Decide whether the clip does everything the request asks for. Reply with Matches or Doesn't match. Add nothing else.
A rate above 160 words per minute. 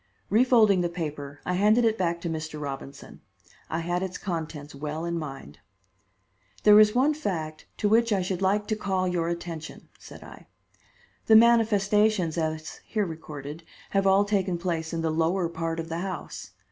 Matches